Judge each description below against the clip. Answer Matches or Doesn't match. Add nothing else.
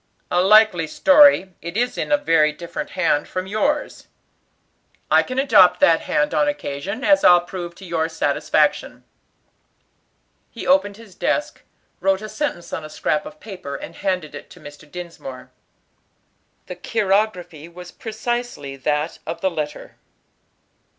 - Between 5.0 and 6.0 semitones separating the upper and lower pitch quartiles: Matches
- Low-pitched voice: Doesn't match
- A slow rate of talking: Doesn't match